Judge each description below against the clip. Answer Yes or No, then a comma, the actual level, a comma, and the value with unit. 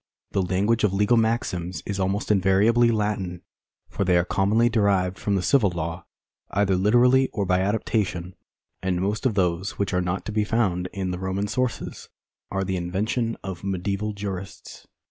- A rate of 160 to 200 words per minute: Yes, average, 170 wpm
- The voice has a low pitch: Yes, very low, 95 Hz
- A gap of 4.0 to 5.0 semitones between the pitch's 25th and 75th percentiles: No, average, 2.7 semitones